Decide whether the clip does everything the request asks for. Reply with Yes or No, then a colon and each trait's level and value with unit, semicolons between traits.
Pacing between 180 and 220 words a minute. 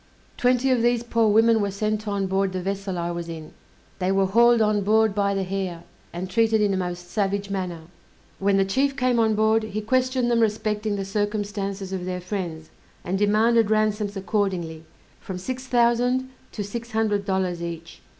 Yes: average, 185 wpm